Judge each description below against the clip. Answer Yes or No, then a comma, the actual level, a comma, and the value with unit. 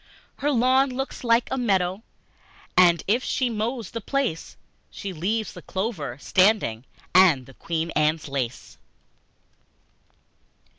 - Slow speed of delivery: Yes, slow, 120 wpm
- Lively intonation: Yes, wide, 6.8 semitones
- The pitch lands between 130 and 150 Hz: No, high, 195 Hz